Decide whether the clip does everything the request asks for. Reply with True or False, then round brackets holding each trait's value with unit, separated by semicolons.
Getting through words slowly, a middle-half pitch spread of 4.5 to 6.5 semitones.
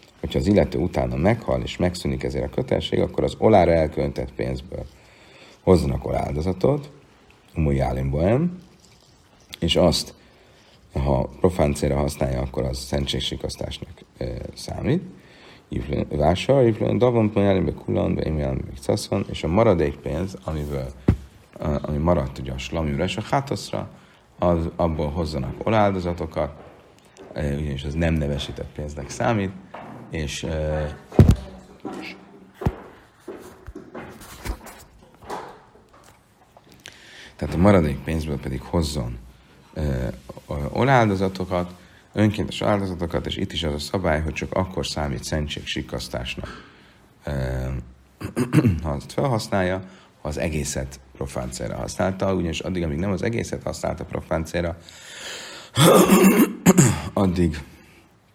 True (100 wpm; 5.2 semitones)